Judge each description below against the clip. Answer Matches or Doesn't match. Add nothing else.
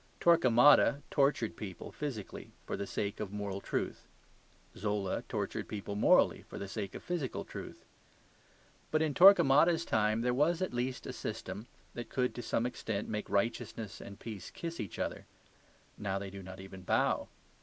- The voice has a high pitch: Doesn't match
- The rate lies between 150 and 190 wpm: Matches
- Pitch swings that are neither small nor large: Doesn't match